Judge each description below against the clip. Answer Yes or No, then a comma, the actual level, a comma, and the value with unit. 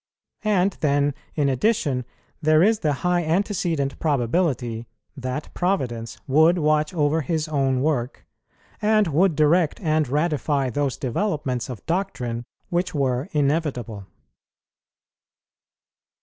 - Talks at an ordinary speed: No, slow, 110 wpm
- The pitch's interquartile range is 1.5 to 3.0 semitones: No, average, 4.7 semitones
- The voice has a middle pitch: Yes, medium, 150 Hz